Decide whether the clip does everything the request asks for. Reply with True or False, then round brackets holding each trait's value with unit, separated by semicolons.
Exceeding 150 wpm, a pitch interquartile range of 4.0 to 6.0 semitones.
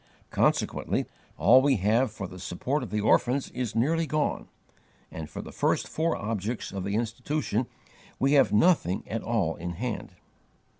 True (160 wpm; 5.1 semitones)